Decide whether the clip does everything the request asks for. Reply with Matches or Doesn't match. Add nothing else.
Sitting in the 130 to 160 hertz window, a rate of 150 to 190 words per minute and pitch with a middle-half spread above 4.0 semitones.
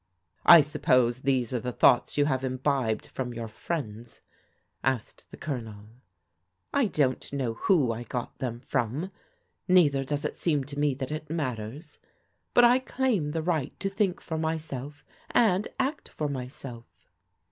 Matches